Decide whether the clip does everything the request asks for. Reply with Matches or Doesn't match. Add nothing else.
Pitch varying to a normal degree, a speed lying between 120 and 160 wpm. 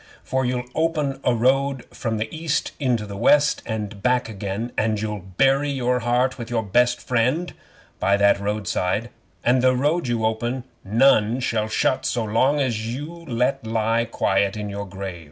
Doesn't match